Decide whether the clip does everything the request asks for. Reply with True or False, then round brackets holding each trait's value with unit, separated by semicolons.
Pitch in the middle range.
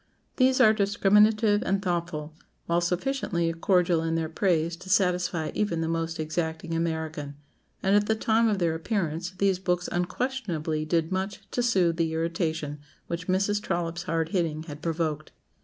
True (175 Hz)